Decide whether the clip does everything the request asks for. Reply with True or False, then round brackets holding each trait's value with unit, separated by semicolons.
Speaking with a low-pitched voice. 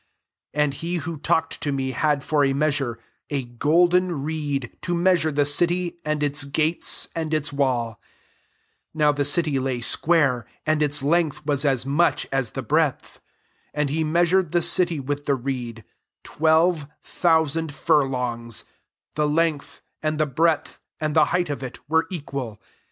False (150 Hz)